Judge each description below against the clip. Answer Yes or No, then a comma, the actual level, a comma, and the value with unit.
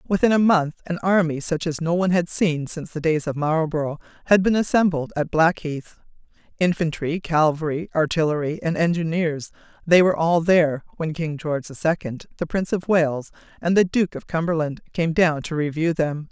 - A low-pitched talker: No, medium, 165 Hz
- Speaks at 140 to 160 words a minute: No, average, 180 wpm